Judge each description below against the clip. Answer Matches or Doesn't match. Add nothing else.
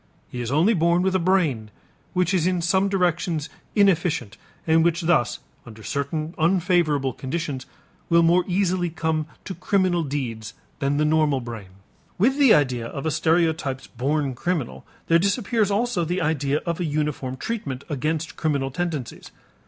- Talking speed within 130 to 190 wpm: Matches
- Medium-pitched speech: Matches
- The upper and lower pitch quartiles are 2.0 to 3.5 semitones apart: Doesn't match